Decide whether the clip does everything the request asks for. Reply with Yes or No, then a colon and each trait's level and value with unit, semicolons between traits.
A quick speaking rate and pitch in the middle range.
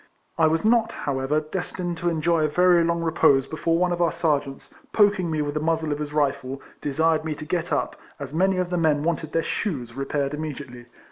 Yes: fast, 215 wpm; medium, 160 Hz